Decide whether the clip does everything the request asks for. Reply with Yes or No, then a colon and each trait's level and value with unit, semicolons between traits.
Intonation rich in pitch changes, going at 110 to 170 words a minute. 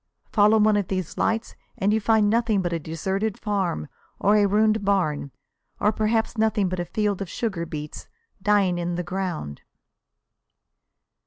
No: average, 3.5 semitones; average, 160 wpm